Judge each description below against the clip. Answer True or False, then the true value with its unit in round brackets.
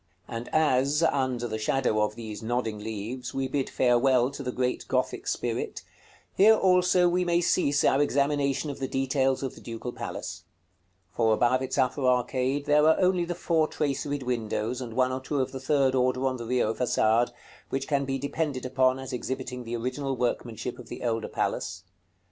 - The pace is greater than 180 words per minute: True (190 wpm)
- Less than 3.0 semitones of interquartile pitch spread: True (2.6 semitones)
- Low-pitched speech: True (130 Hz)